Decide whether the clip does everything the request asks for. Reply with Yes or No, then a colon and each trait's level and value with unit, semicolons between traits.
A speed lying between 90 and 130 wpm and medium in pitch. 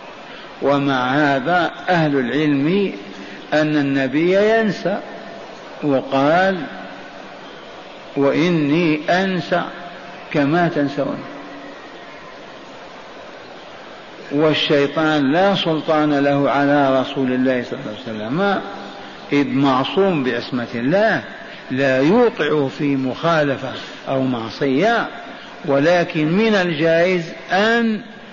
No: average, 80 wpm; medium, 150 Hz